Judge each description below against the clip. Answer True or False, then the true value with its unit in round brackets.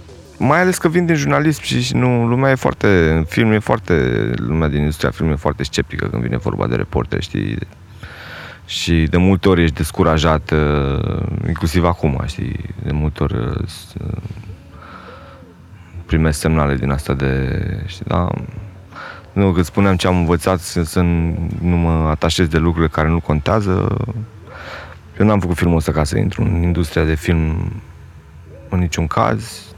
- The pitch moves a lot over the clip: False (4.0 semitones)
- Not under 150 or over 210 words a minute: True (155 wpm)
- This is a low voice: True (85 Hz)